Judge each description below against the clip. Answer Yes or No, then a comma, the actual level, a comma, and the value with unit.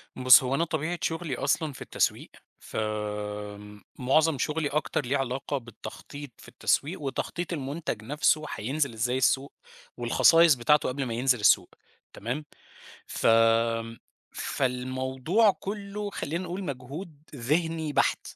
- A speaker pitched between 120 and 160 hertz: Yes, medium, 140 Hz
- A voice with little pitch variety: No, average, 4.4 semitones